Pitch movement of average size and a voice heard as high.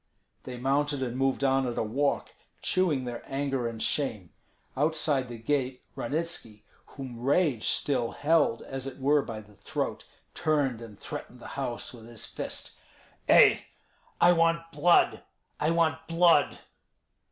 No: average, 4.0 semitones; low, 135 Hz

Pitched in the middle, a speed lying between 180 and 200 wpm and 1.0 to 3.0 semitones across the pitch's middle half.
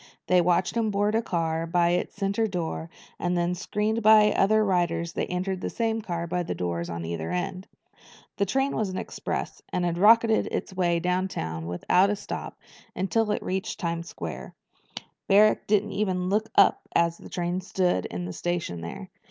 No: medium, 180 Hz; average, 185 wpm; average, 3.5 semitones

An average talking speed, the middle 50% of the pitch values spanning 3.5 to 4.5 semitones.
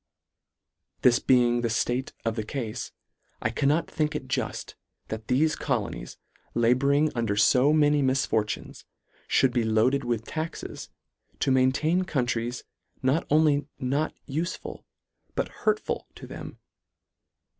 No: slow, 125 wpm; average, 3.9 semitones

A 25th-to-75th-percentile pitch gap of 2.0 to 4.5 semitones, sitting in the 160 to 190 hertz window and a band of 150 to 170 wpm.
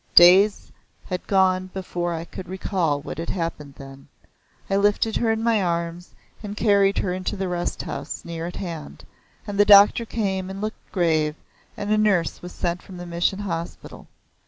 No: average, 3.0 semitones; medium, 185 Hz; average, 180 wpm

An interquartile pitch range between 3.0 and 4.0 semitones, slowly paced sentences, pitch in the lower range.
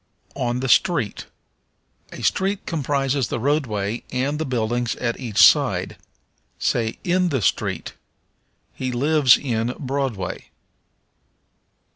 Yes: average, 3.6 semitones; slow, 110 wpm; low, 130 Hz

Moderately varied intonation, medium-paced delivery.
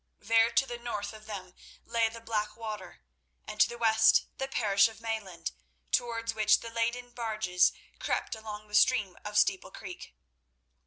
No: narrow, 1.8 semitones; average, 160 wpm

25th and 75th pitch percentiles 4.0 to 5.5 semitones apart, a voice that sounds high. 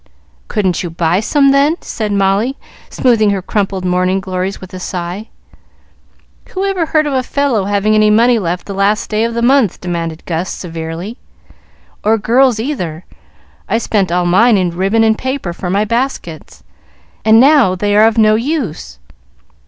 Yes: average, 4.4 semitones; high, 210 Hz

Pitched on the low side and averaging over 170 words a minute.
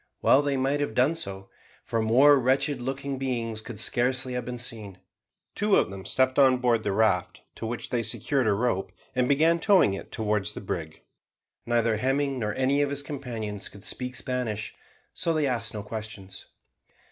Yes: low, 125 Hz; average, 180 wpm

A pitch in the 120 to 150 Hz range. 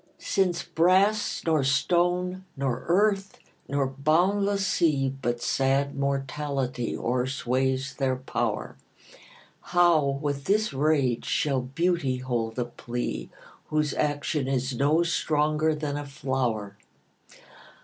Yes: medium, 140 Hz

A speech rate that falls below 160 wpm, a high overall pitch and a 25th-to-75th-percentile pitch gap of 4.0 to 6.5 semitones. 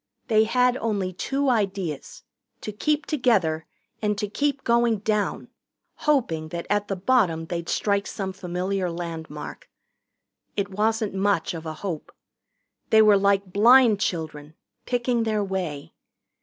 Yes: slow, 135 wpm; high, 200 Hz; average, 4.4 semitones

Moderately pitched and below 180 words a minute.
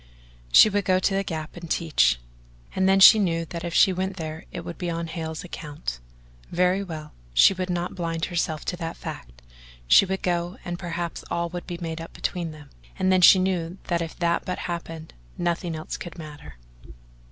No: medium, 170 Hz; average, 200 wpm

